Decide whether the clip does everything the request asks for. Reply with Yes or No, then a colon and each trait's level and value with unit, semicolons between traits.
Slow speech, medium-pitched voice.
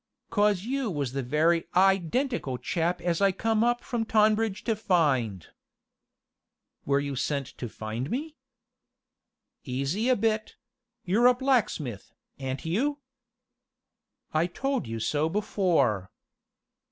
Yes: slow, 125 wpm; medium, 180 Hz